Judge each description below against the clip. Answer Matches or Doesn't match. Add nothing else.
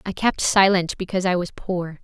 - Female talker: Matches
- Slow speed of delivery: Doesn't match